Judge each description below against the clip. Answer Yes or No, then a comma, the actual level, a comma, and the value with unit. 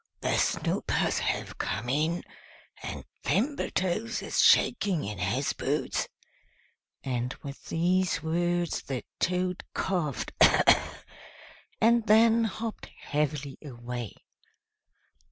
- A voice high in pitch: No, medium, 170 Hz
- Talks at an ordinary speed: No, slow, 95 wpm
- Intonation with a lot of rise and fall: Yes, wide, 6.0 semitones